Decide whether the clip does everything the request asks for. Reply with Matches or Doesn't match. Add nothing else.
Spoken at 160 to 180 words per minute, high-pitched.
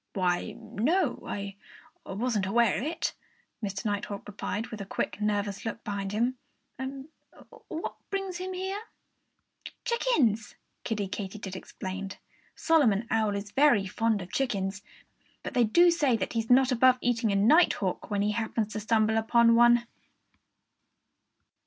Doesn't match